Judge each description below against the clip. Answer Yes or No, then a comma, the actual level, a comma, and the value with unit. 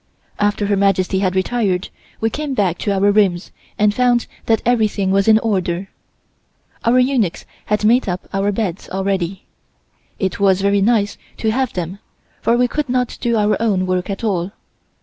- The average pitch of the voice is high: Yes, high, 205 Hz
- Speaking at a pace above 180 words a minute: No, average, 170 wpm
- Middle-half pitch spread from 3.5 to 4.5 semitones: No, average, 3.1 semitones